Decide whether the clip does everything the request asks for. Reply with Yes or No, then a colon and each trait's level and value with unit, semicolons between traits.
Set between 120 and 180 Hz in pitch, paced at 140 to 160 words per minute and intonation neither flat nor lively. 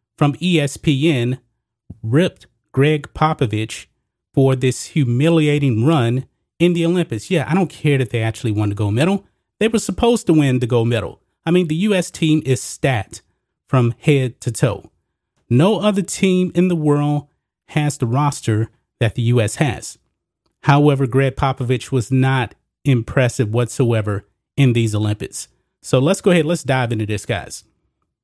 Yes: low, 135 Hz; average, 155 wpm; average, 4.9 semitones